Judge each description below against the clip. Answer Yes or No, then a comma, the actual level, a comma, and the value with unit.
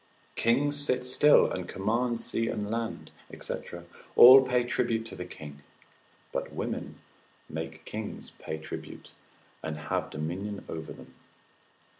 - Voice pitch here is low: Yes, low, 110 Hz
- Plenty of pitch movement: Yes, wide, 7.2 semitones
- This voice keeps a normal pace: No, slow, 130 wpm